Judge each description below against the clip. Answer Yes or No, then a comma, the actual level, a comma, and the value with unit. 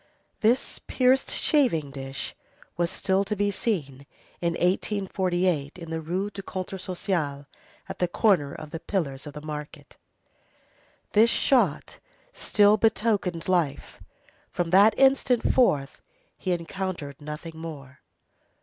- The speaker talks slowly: Yes, slow, 125 wpm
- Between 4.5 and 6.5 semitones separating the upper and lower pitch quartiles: Yes, average, 5.1 semitones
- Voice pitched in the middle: Yes, medium, 180 Hz